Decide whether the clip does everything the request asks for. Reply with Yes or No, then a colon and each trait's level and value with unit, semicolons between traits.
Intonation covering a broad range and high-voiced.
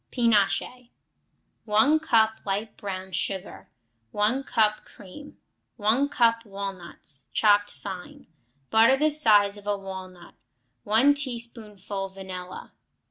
No: average, 3.3 semitones; high, 210 Hz